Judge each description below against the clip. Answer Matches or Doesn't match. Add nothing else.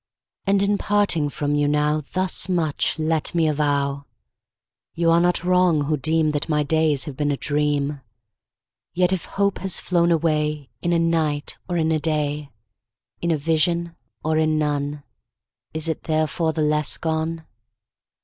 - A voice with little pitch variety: Matches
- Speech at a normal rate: Matches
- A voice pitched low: Doesn't match